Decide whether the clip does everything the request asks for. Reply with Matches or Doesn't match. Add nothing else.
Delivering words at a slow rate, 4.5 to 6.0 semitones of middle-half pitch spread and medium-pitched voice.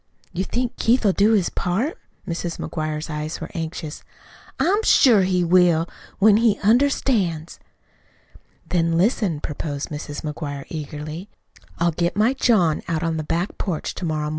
Doesn't match